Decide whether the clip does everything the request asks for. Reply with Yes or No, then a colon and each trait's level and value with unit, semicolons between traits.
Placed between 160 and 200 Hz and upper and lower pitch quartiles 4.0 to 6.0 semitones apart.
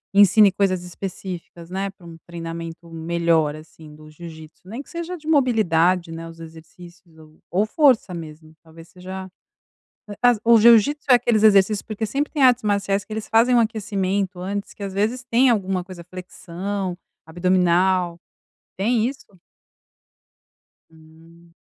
Yes: medium, 185 Hz; average, 4.4 semitones